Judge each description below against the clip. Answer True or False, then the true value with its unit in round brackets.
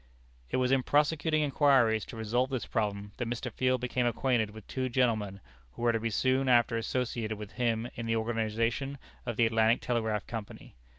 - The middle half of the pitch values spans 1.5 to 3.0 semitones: True (2.5 semitones)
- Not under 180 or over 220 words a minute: True (185 wpm)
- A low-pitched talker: True (120 Hz)